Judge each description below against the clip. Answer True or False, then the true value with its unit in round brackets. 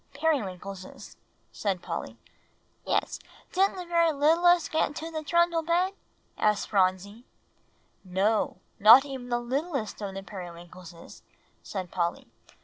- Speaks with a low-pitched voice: False (240 Hz)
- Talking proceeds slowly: True (120 wpm)